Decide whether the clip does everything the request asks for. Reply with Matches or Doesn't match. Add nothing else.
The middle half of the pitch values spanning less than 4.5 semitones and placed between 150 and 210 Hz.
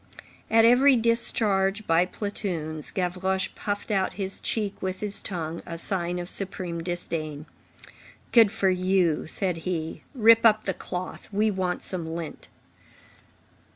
Matches